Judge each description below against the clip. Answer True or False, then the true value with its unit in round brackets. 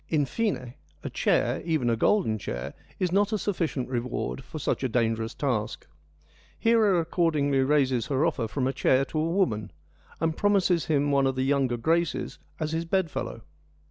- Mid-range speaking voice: True (145 Hz)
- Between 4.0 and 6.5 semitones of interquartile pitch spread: True (5.0 semitones)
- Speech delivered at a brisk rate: False (175 wpm)